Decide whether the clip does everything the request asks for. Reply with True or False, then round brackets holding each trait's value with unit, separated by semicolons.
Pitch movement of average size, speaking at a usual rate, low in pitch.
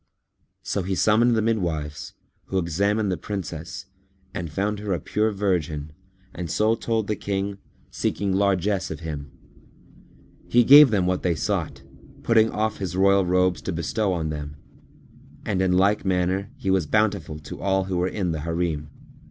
True (3.6 semitones; 165 wpm; 95 Hz)